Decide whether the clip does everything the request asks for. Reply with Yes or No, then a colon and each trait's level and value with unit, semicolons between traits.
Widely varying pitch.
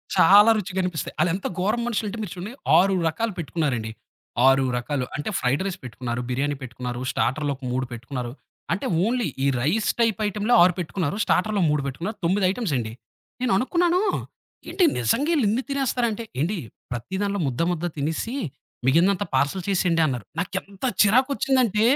Yes: wide, 7.4 semitones